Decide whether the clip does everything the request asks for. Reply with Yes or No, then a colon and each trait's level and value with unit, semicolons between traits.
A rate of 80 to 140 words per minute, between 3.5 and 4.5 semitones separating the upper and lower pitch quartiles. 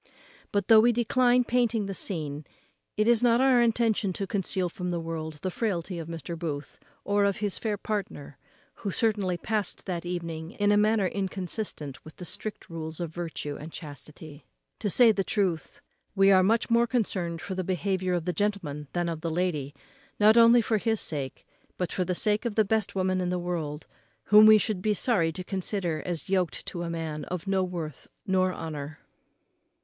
No: average, 195 wpm; average, 4.2 semitones